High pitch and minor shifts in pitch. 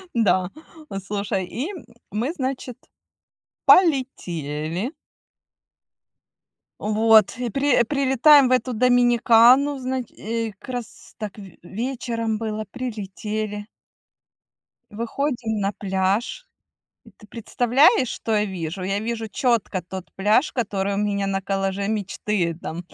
No: high, 220 Hz; average, 4.0 semitones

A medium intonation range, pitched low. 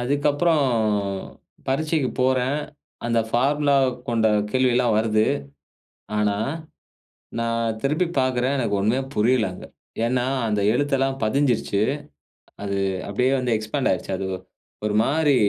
Yes: average, 3.7 semitones; low, 125 Hz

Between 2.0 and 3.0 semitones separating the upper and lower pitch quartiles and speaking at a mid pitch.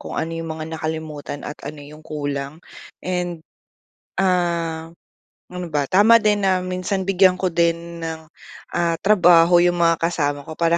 Yes: narrow, 2.4 semitones; medium, 170 Hz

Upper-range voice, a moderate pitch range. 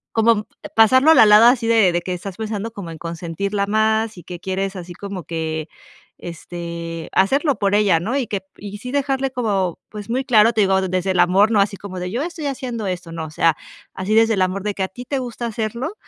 Yes: high, 200 Hz; average, 4.1 semitones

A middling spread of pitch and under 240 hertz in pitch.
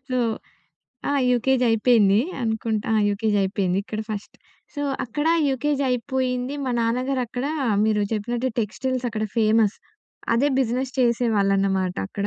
Yes: average, 3.4 semitones; high, 230 Hz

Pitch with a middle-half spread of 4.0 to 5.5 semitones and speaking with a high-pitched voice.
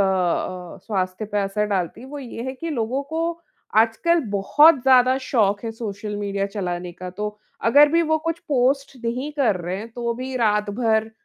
Yes: average, 5.1 semitones; high, 225 Hz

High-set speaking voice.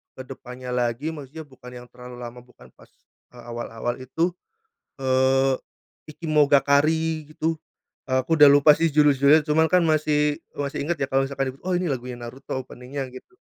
No: low, 135 Hz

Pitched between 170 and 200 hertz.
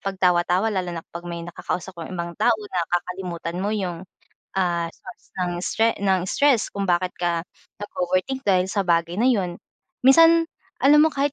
Yes: medium, 185 Hz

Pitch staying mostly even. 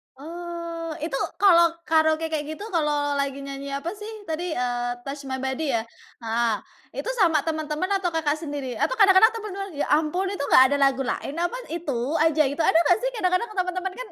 No: average, 4.4 semitones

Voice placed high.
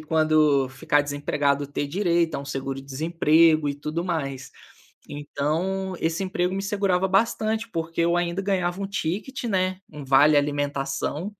No: medium, 165 Hz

